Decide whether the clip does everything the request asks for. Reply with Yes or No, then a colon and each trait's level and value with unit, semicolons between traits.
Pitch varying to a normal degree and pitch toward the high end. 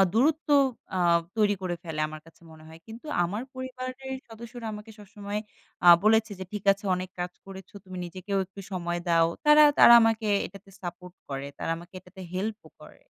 Yes: average, 4.1 semitones; high, 200 Hz